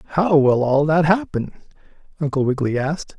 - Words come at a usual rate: Yes, average, 150 wpm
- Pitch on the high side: No, medium, 150 Hz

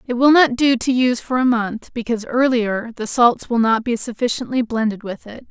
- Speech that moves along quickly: Yes, fast, 220 wpm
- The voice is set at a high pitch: Yes, high, 240 Hz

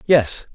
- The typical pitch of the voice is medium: Yes, medium, 145 Hz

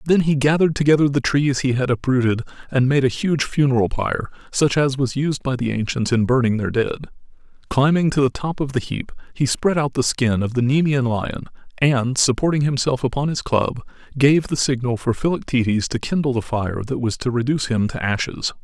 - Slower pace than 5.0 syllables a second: No, 5.5 syllables/s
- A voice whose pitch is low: Yes, low, 130 Hz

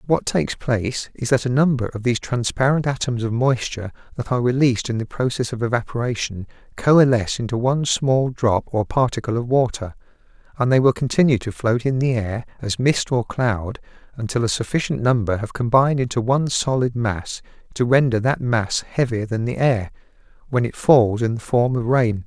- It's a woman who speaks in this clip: No, male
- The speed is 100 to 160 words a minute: No, average, 185 wpm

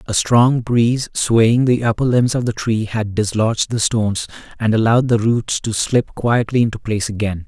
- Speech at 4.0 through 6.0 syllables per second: Yes, 5.0 syllables/s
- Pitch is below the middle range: Yes, low, 115 Hz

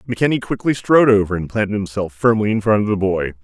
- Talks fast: Yes, fast, 225 wpm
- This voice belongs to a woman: No, male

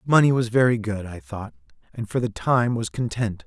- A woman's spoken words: No, male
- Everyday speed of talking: No, fast, 210 wpm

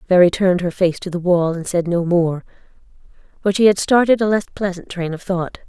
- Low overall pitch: No, medium, 180 Hz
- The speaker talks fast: Yes, fast, 220 wpm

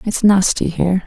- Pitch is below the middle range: No, high, 190 Hz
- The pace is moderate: Yes, average, 170 wpm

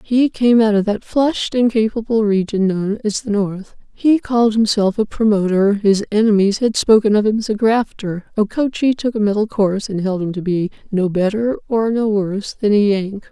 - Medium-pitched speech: No, high, 210 Hz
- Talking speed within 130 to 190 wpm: No, fast, 205 wpm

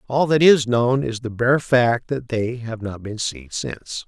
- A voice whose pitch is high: No, low, 120 Hz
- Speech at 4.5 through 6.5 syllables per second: No, 4.2 syllables/s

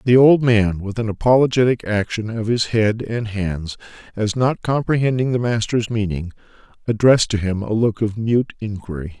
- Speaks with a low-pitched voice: Yes, low, 110 Hz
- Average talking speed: Yes, average, 170 wpm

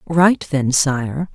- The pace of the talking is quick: No, slow, 135 wpm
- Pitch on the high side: No, medium, 150 Hz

